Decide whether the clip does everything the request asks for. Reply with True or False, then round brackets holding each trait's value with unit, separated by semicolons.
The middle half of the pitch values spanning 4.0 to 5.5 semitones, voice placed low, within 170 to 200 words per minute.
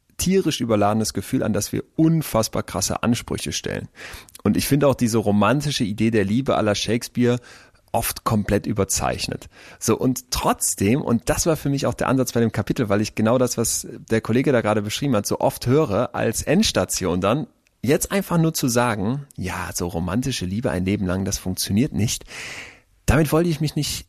True (4.8 semitones; 115 Hz; 185 wpm)